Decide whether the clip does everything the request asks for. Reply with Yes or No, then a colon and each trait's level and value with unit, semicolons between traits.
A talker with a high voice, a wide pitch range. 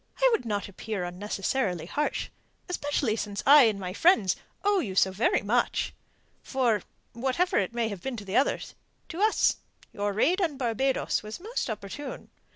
Yes: high, 230 Hz; wide, 6.4 semitones